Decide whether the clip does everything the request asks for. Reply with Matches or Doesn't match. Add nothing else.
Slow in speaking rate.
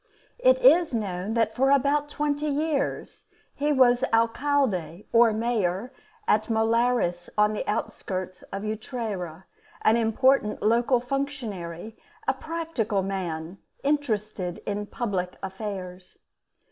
Matches